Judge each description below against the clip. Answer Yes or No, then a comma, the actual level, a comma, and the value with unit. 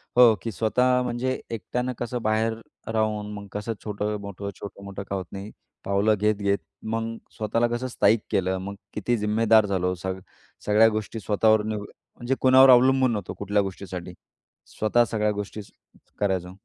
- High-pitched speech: No, low, 105 Hz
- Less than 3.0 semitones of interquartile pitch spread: Yes, narrow, 2.4 semitones